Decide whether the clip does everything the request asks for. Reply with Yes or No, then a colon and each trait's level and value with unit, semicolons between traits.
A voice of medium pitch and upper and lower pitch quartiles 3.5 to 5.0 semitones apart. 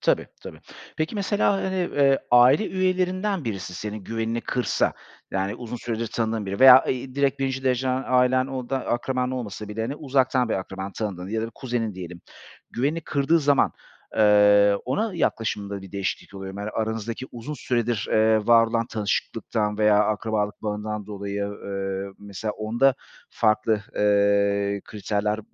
No: low, 110 Hz; average, 4.1 semitones